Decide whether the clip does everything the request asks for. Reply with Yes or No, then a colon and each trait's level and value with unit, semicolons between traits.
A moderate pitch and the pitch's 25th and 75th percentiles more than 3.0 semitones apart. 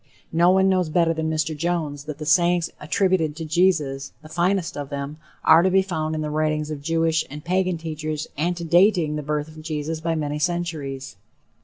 No: medium, 160 Hz; narrow, 2.4 semitones